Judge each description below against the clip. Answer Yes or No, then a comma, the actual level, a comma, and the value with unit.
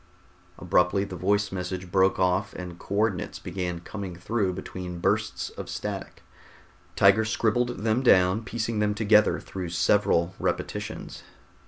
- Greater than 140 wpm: No, slow, 135 wpm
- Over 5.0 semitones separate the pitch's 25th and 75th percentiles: No, average, 2.8 semitones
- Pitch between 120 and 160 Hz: No, very low, 95 Hz